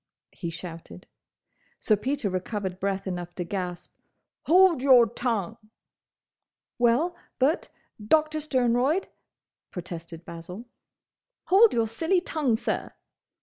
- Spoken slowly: Yes, slow, 105 wpm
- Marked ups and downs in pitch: Yes, wide, 8.3 semitones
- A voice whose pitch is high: Yes, high, 225 Hz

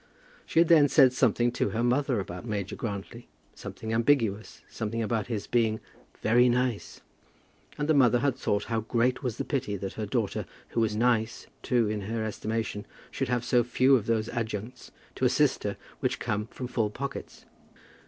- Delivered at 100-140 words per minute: No, average, 180 wpm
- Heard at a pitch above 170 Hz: No, low, 115 Hz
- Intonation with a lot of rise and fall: No, narrow, 2.5 semitones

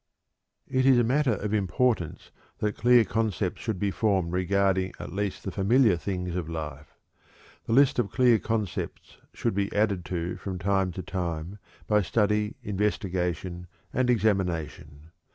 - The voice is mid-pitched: No, low, 100 Hz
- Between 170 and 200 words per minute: No, average, 150 wpm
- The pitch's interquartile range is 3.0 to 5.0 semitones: Yes, average, 3.5 semitones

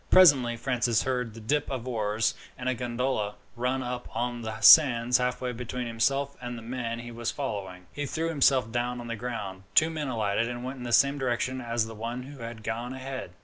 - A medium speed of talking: No, fast, 210 wpm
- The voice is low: Yes, low, 120 Hz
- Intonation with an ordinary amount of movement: No, narrow, 2.1 semitones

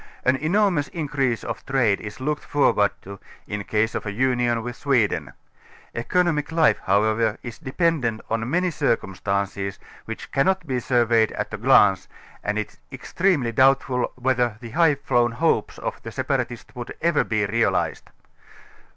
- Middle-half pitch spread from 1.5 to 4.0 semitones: No, average, 4.7 semitones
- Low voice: Yes, low, 125 Hz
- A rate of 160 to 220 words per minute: No, average, 150 wpm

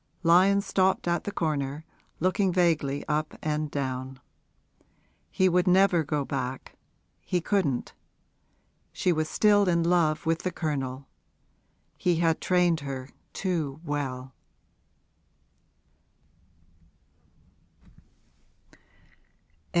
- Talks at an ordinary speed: No, slow, 95 wpm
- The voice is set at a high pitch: No, medium, 160 Hz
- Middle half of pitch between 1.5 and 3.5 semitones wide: No, average, 4.2 semitones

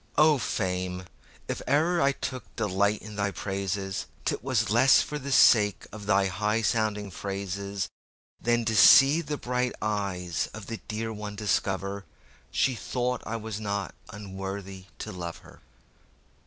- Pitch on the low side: Yes, low, 105 Hz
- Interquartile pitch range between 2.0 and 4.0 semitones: Yes, average, 3.3 semitones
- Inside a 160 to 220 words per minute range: No, average, 140 wpm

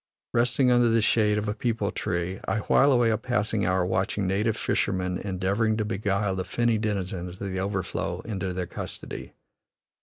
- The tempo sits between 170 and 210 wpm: Yes, average, 175 wpm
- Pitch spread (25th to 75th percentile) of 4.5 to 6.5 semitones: No, average, 3.2 semitones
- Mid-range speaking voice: No, low, 105 Hz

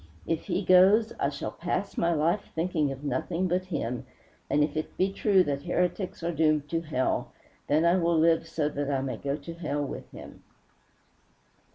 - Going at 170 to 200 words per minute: Yes, average, 190 wpm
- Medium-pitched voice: Yes, medium, 165 Hz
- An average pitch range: Yes, average, 3.6 semitones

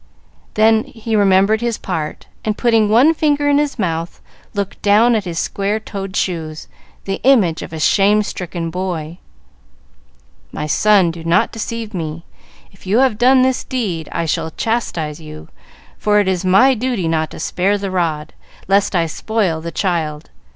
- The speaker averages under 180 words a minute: Yes, average, 165 wpm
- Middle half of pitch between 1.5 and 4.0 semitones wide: No, average, 5.0 semitones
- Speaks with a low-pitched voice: No, high, 195 Hz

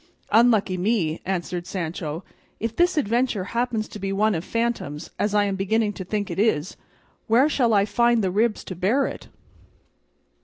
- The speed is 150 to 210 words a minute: Yes, average, 170 wpm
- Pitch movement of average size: Yes, average, 3.8 semitones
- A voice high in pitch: Yes, high, 210 Hz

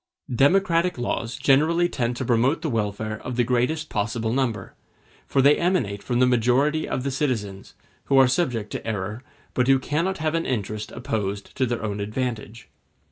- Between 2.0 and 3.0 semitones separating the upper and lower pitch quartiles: No, average, 4.7 semitones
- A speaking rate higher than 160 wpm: Yes, average, 175 wpm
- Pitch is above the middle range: No, low, 125 Hz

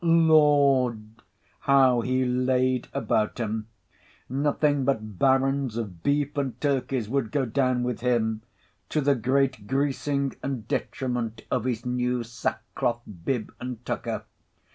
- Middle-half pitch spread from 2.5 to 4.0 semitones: Yes, average, 3.1 semitones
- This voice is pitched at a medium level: No, low, 125 Hz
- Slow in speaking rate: Yes, slow, 120 wpm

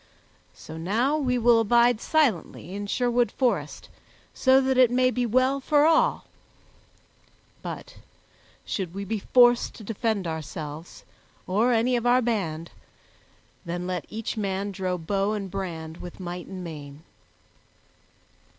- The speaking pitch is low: No, high, 210 Hz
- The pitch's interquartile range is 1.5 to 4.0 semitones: No, wide, 5.6 semitones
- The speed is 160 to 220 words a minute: No, slow, 135 wpm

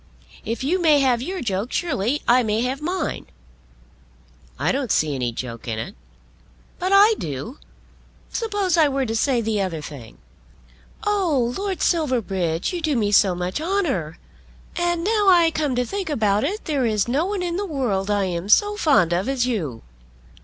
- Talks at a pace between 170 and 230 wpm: Yes, average, 175 wpm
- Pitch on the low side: No, very high, 255 Hz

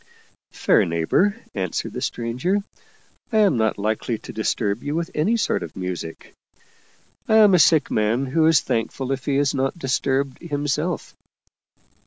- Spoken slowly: No, average, 165 wpm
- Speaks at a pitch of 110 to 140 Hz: Yes, low, 135 Hz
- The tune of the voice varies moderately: No, wide, 6.9 semitones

